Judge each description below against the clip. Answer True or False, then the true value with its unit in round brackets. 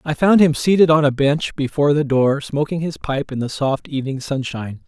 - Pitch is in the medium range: True (145 Hz)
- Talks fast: True (220 wpm)